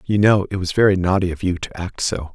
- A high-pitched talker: No, very low, 95 Hz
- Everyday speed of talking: No, fast, 280 wpm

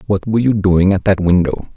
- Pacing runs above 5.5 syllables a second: Yes, 6.4 syllables/s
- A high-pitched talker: No, very low, 95 Hz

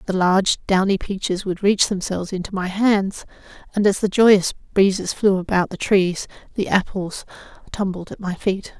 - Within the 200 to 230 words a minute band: No, average, 170 wpm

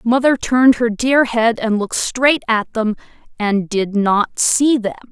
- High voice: Yes, high, 235 Hz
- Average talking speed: Yes, average, 175 wpm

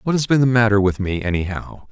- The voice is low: Yes, low, 110 Hz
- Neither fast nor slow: No, fast, 250 wpm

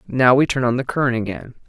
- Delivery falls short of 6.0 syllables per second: No, 6.3 syllables/s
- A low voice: Yes, low, 125 Hz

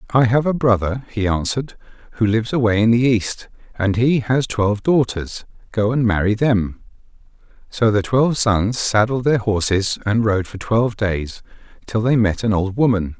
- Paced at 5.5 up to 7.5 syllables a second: No, 4.9 syllables/s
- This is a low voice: Yes, low, 110 Hz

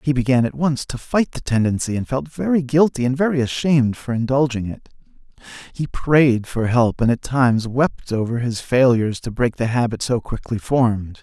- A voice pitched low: Yes, low, 125 Hz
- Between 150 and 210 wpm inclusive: Yes, average, 190 wpm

